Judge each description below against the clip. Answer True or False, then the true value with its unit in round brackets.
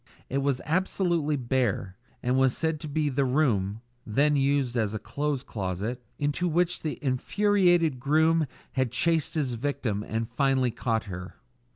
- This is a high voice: False (135 Hz)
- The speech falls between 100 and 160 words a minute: True (155 wpm)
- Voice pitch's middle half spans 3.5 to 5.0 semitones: True (4.6 semitones)